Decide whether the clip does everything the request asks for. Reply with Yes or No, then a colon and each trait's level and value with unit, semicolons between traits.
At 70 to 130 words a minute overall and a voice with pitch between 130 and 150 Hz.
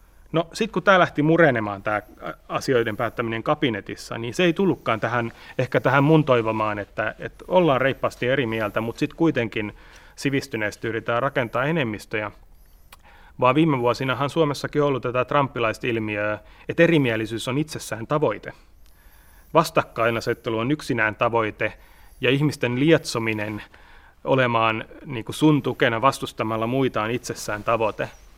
No: average, 125 wpm; low, 120 Hz